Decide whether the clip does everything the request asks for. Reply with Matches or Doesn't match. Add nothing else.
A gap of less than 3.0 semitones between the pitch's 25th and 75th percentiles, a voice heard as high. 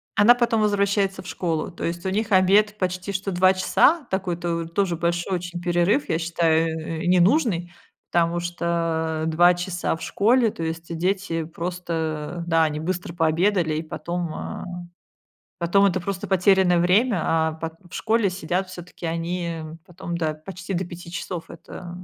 Doesn't match